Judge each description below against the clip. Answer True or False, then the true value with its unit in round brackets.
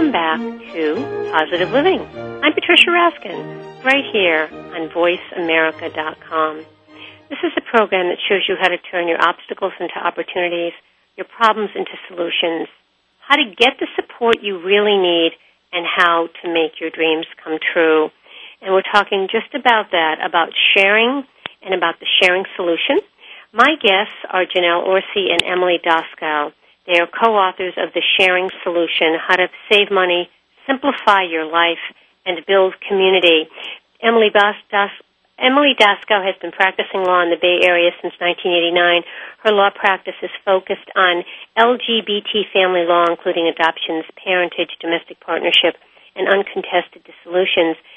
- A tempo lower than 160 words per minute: True (140 wpm)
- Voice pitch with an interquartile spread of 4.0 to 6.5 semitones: False (3.4 semitones)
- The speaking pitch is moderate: True (180 Hz)